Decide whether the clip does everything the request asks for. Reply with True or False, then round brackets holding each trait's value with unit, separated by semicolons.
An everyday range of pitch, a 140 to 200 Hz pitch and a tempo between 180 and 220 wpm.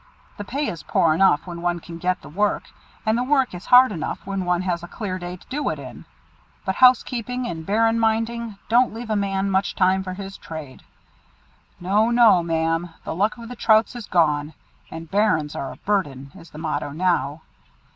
True (5.0 semitones; 190 Hz; 200 wpm)